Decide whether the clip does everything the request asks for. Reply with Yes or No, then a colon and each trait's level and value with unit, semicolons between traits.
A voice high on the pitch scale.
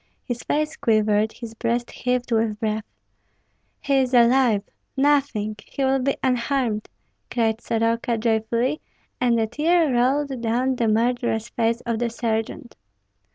Yes: high, 235 Hz